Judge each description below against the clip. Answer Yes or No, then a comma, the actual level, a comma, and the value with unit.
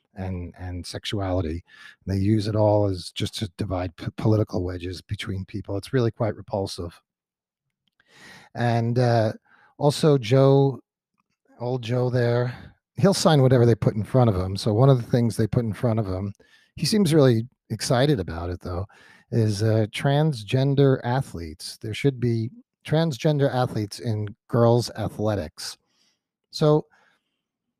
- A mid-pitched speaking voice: No, low, 115 Hz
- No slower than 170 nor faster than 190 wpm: No, average, 145 wpm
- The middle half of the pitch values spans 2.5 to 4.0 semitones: No, average, 4.7 semitones